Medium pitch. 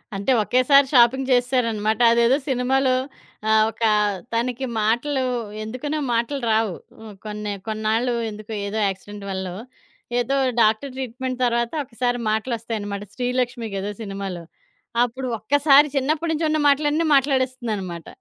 No: high, 240 Hz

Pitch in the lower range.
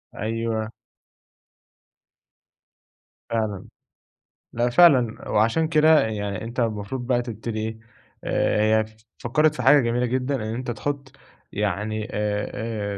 Yes: low, 115 Hz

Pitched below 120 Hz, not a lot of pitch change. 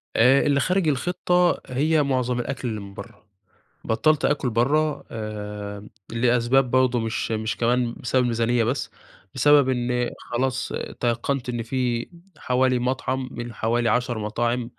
No: low, 125 Hz; narrow, 2.3 semitones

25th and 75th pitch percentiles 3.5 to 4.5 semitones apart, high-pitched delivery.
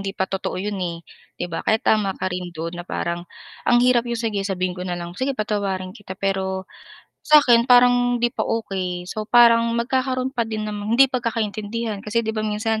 Yes: average, 3.8 semitones; high, 215 Hz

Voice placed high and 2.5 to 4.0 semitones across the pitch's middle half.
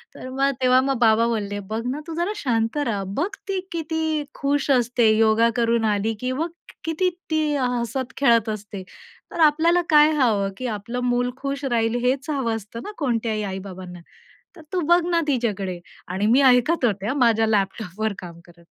No: high, 240 Hz; average, 4.7 semitones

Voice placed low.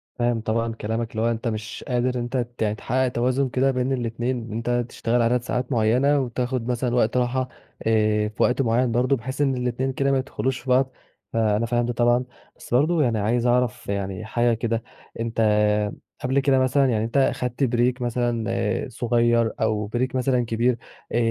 Yes: low, 120 Hz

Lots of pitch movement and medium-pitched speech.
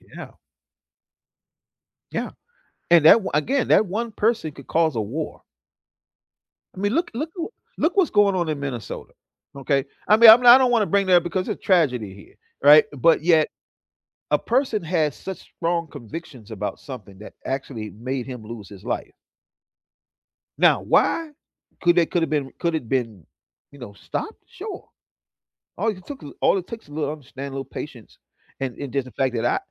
Yes: wide, 7.8 semitones; medium, 155 Hz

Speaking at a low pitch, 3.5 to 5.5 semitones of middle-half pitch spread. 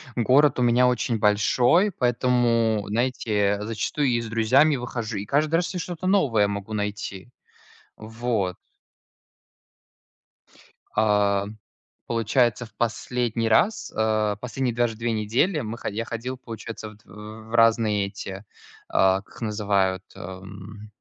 No: low, 115 Hz; average, 2.9 semitones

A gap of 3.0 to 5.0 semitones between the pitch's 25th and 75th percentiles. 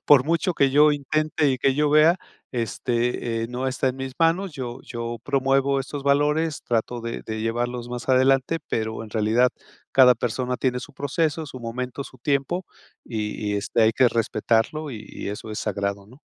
Yes: average, 3.5 semitones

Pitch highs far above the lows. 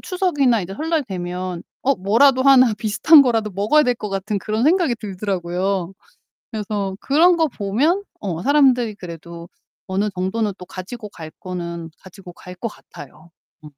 Yes: wide, 5.9 semitones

